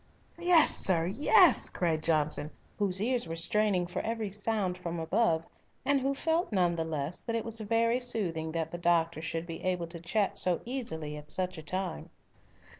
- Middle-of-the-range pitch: Yes, medium, 180 Hz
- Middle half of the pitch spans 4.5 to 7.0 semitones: Yes, wide, 5.5 semitones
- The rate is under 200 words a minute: Yes, average, 185 wpm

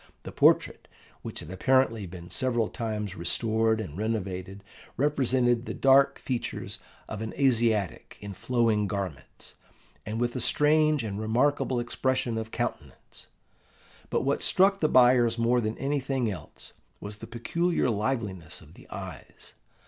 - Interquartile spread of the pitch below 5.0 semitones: Yes, average, 3.8 semitones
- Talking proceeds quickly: No, average, 140 wpm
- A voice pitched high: No, low, 115 Hz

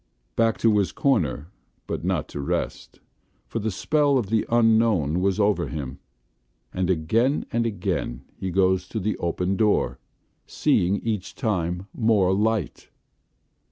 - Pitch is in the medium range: No, low, 100 Hz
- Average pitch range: Yes, average, 4.2 semitones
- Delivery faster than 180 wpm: No, average, 140 wpm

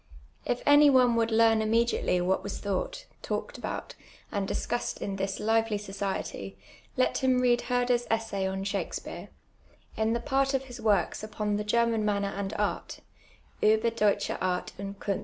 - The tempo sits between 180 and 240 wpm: No, average, 165 wpm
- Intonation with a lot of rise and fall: No, average, 3.0 semitones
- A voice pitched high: Yes, high, 220 Hz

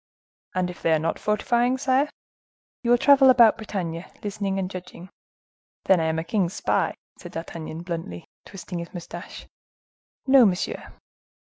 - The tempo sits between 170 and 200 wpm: No, average, 150 wpm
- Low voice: No, medium, 185 Hz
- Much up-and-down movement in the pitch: Yes, wide, 5.8 semitones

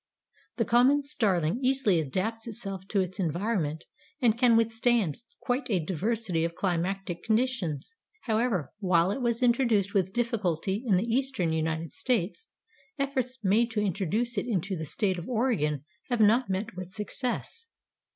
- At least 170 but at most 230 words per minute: No, average, 150 wpm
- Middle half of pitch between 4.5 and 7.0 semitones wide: Yes, average, 4.9 semitones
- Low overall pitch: No, high, 210 Hz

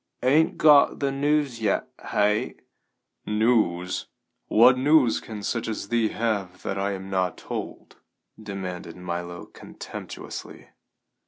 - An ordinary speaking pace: No, slow, 115 wpm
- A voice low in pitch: Yes, low, 105 Hz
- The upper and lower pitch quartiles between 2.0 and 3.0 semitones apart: No, average, 5.1 semitones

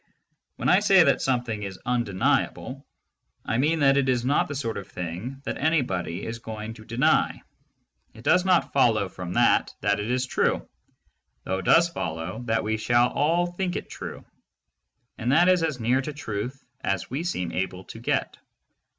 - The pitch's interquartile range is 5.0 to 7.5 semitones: Yes, wide, 5.6 semitones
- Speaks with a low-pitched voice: Yes, low, 120 Hz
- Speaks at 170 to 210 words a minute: Yes, average, 185 wpm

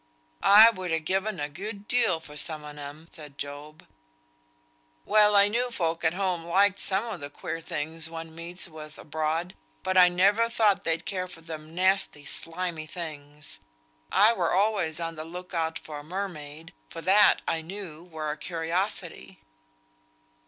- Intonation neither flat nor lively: Yes, average, 3.5 semitones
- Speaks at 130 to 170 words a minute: Yes, average, 165 wpm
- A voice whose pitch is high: No, medium, 165 Hz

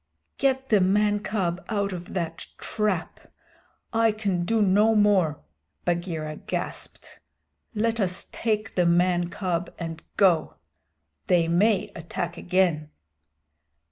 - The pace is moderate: No, slow, 115 wpm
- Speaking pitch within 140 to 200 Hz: Yes, medium, 185 Hz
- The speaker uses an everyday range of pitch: Yes, average, 3.5 semitones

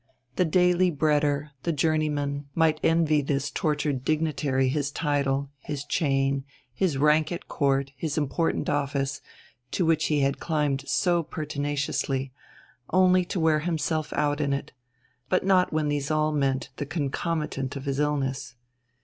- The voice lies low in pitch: No, medium, 145 Hz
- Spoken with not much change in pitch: Yes, narrow, 2.3 semitones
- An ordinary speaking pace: Yes, average, 145 wpm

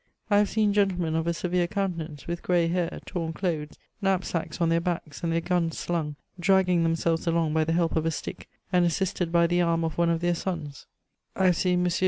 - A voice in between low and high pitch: Yes, medium, 170 Hz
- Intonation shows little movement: Yes, narrow, 1.6 semitones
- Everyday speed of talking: No, fast, 225 wpm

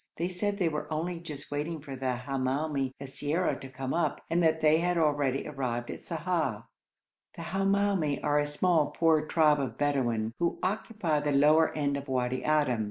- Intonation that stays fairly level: No, average, 3.6 semitones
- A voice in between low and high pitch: Yes, medium, 150 Hz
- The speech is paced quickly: No, average, 180 wpm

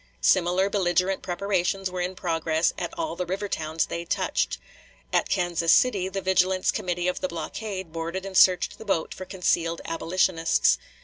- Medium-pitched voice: Yes, medium, 180 Hz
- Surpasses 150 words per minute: Yes, average, 165 wpm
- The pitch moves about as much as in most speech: No, narrow, 2.0 semitones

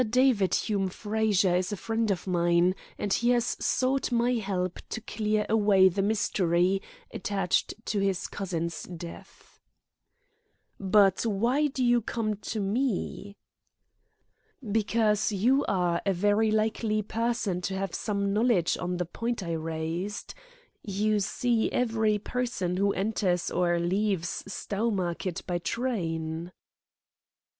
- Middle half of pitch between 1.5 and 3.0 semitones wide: No, average, 3.5 semitones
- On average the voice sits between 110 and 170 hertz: No, high, 200 Hz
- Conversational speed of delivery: No, slow, 125 wpm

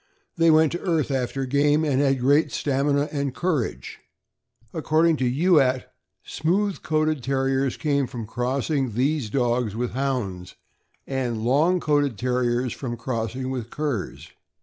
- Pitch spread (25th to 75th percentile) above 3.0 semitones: Yes, average, 3.5 semitones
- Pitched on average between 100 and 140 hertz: Yes, low, 135 Hz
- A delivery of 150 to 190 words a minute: No, slow, 135 wpm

